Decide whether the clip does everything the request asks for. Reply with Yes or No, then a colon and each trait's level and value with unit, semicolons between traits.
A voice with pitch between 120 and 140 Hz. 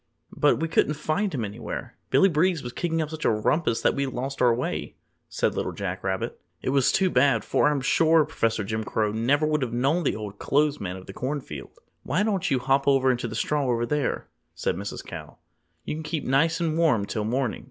Yes: low, 135 Hz